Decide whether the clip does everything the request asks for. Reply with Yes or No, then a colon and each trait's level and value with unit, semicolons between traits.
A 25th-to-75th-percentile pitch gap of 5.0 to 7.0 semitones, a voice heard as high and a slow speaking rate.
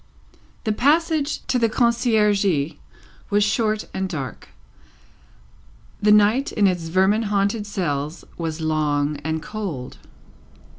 Yes: wide, 5.4 semitones; high, 205 Hz; slow, 110 wpm